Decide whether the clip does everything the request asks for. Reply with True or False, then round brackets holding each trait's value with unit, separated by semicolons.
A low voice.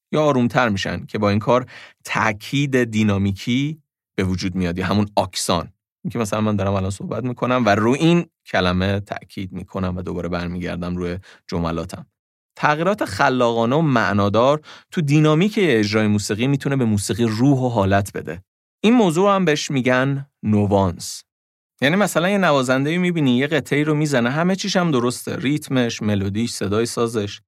True (115 Hz)